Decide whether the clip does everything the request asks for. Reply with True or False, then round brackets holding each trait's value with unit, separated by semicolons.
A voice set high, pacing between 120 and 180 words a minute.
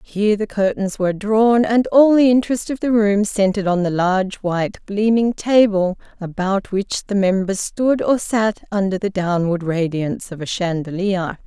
True (200 Hz; 175 wpm)